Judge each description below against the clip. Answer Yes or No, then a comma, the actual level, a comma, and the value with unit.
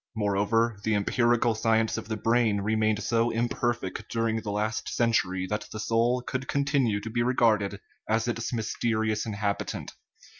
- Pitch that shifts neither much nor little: No, narrow, 1.8 semitones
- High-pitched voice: No, low, 110 Hz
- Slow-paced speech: No, average, 160 wpm